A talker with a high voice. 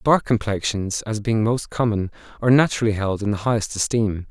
No: low, 110 Hz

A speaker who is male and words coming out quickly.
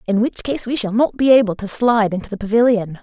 No: female; fast, 260 wpm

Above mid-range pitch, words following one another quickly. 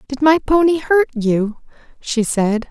No: very high, 265 Hz; average, 155 wpm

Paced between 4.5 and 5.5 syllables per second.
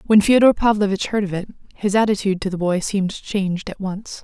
No: 6.0 syllables/s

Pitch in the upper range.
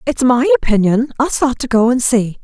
Yes: high, 235 Hz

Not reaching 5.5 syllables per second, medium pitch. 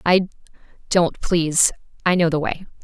Yes: 4.9 syllables/s; medium, 170 Hz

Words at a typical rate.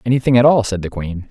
No: fast, 275 wpm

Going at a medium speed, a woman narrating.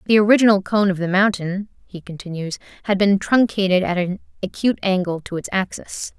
Yes: average, 175 wpm; female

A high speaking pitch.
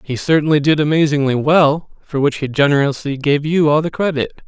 No: medium, 145 Hz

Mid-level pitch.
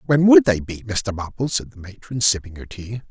No: low, 115 Hz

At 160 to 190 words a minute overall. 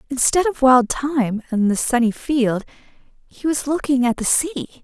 Yes: average, 175 wpm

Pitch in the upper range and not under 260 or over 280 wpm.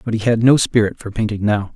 No: low, 110 Hz; fast, 275 wpm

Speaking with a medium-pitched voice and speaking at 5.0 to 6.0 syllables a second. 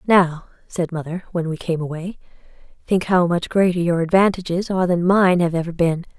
Yes: medium, 175 Hz; 5.4 syllables/s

